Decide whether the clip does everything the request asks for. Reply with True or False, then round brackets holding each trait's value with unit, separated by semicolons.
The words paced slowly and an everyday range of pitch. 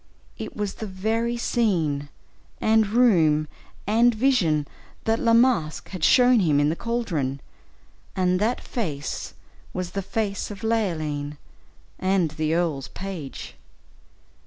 False (125 wpm; 6.5 semitones)